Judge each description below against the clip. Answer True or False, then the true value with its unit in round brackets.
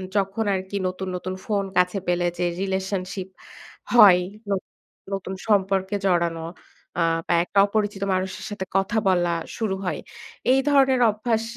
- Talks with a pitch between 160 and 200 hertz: True (190 Hz)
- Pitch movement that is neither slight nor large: False (2.0 semitones)